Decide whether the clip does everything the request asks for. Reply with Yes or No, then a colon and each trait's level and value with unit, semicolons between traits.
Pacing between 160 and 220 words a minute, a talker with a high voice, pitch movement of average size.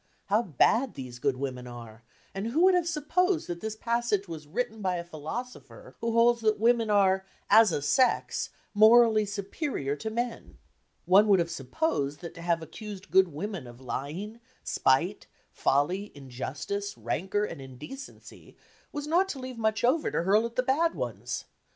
No: average, 170 wpm; high, 205 Hz; wide, 6.9 semitones